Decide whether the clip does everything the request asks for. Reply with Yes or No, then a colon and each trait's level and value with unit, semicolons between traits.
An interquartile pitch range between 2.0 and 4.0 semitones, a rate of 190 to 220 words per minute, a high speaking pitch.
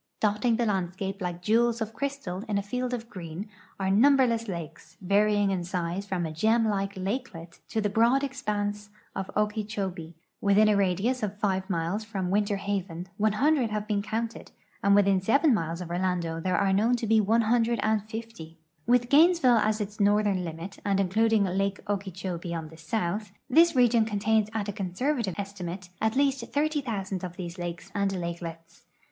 No: average, 3.4 semitones; average, 170 wpm; high, 205 Hz